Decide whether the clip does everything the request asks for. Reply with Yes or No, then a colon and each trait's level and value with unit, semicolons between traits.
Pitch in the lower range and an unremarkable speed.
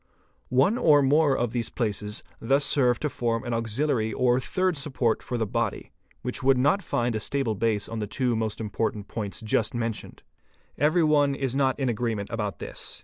Yes: low, 120 Hz; average, 190 wpm